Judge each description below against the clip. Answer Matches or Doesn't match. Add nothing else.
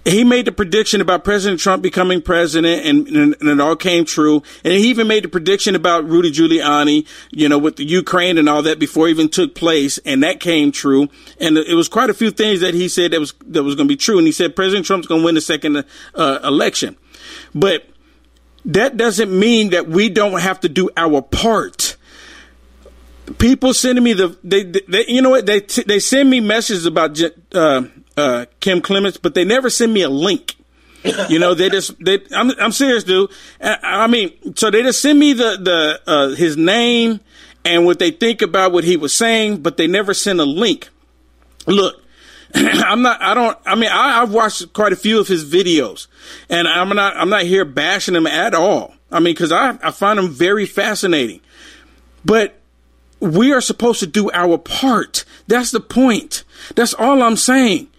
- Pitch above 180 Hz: Matches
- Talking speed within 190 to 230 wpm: Matches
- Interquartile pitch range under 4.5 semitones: Doesn't match